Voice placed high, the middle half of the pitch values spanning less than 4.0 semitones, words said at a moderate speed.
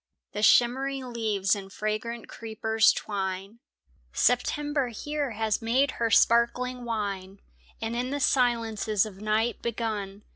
No: high, 225 Hz; average, 2.8 semitones; slow, 120 wpm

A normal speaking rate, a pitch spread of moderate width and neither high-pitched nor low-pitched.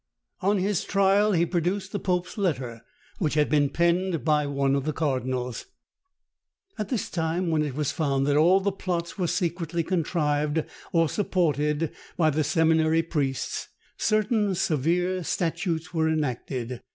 Yes: average, 150 wpm; average, 3.7 semitones; medium, 165 Hz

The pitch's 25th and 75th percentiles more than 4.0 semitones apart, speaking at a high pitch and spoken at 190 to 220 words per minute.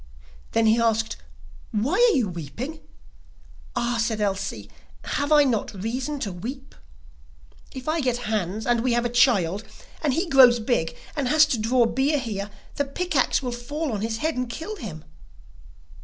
No: average, 4.4 semitones; high, 240 Hz; average, 170 wpm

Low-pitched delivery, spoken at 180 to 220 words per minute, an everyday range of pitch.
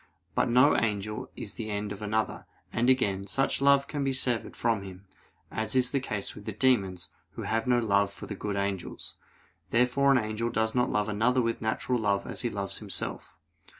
Yes: low, 110 Hz; average, 200 wpm; average, 3.5 semitones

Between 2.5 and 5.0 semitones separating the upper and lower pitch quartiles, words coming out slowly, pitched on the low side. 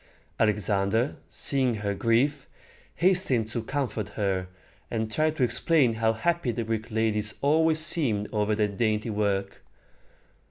Yes: average, 4.6 semitones; slow, 130 wpm; low, 110 Hz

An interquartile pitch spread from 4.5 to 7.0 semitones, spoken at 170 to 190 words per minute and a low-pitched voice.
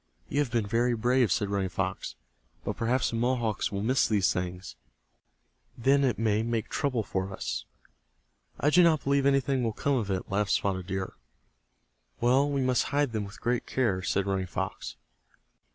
Yes: average, 4.8 semitones; average, 175 wpm; low, 115 Hz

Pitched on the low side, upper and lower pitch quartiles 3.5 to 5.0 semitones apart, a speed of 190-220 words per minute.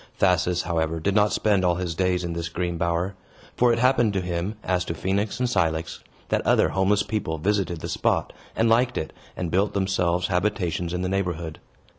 No: very low, 90 Hz; average, 3.1 semitones; average, 195 wpm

